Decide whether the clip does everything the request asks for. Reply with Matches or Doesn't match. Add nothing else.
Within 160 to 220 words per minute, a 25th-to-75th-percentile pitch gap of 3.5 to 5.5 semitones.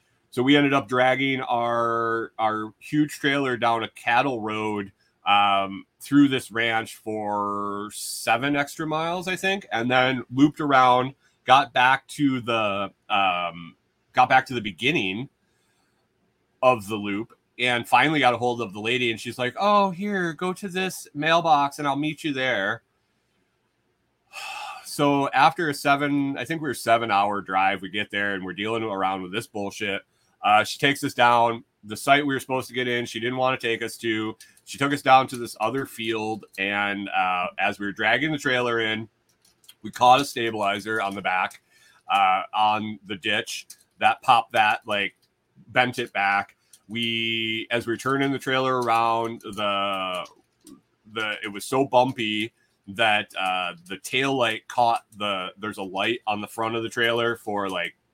Matches